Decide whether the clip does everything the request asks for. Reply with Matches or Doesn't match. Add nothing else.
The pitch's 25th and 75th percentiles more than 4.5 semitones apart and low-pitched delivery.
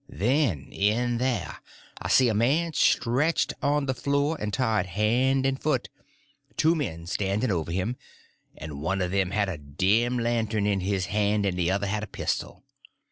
Matches